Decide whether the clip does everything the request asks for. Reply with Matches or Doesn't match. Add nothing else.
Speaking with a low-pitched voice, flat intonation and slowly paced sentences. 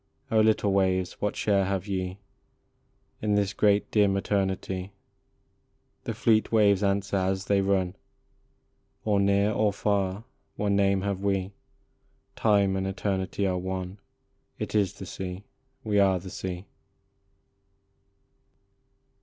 Matches